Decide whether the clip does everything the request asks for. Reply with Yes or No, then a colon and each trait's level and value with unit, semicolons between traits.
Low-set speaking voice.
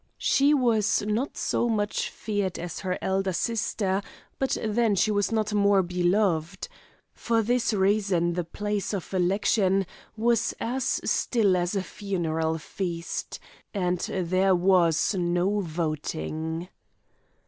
No: high, 195 Hz